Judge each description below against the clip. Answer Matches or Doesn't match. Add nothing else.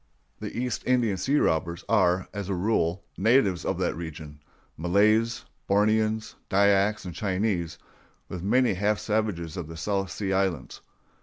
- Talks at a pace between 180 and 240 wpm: Doesn't match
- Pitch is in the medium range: Doesn't match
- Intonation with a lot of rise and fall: Doesn't match